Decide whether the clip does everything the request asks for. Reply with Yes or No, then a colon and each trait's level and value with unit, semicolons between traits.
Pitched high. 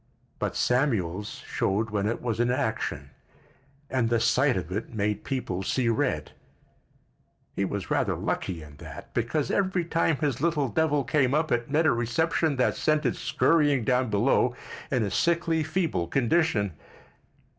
No: low, 125 Hz